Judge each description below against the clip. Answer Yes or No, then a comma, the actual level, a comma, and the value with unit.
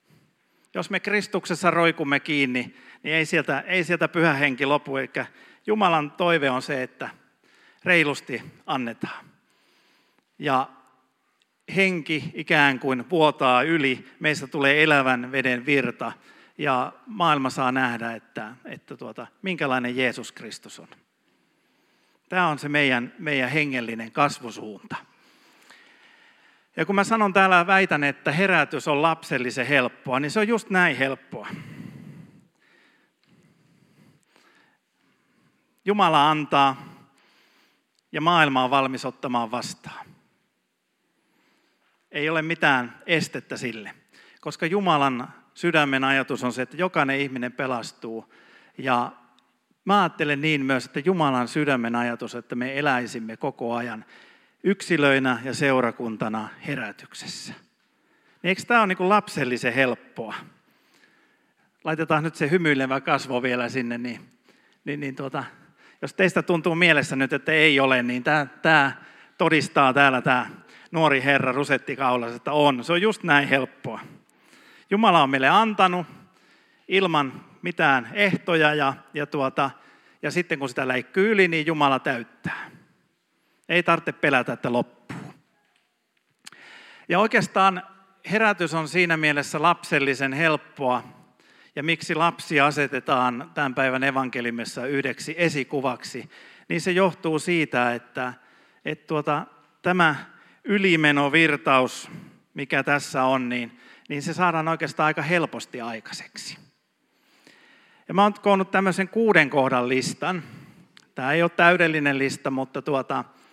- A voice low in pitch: No, medium, 145 Hz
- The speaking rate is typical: Yes, average, 120 wpm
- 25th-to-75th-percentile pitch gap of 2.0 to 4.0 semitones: No, average, 4.5 semitones